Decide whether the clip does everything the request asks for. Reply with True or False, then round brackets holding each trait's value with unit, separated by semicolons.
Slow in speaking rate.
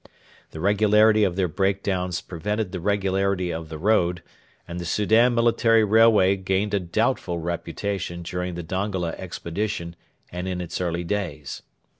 False (150 wpm)